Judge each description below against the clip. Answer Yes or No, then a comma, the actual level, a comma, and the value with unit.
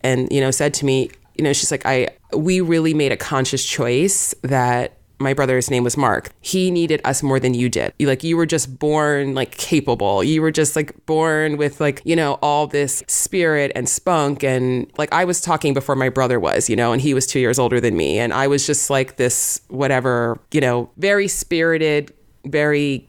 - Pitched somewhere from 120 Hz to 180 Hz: Yes, medium, 140 Hz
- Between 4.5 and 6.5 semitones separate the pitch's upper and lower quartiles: No, average, 3.0 semitones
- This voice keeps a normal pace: No, fast, 215 wpm